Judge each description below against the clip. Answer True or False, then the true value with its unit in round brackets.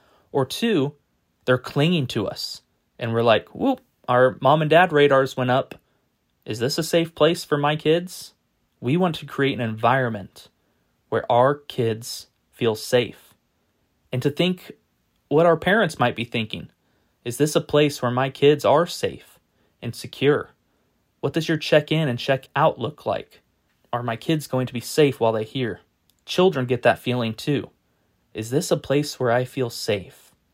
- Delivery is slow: False (175 wpm)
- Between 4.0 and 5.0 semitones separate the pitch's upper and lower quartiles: True (4.4 semitones)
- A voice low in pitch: True (130 Hz)